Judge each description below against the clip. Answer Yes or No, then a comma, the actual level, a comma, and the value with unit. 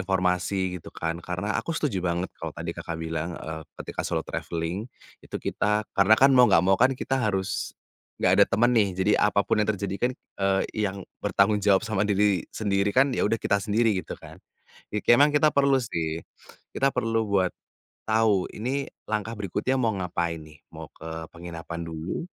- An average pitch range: Yes, average, 3.9 semitones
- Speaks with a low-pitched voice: Yes, low, 100 Hz